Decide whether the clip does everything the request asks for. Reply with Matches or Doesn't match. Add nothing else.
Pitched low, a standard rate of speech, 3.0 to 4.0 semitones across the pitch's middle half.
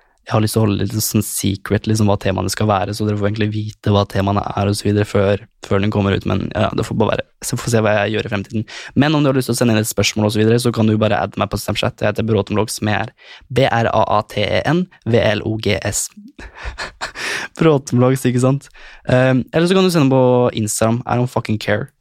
Doesn't match